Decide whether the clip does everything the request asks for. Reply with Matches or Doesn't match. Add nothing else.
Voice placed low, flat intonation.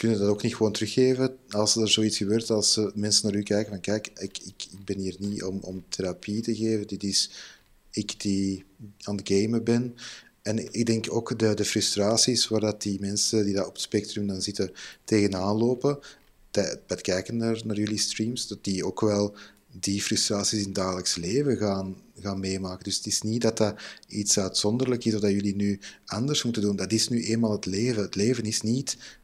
Matches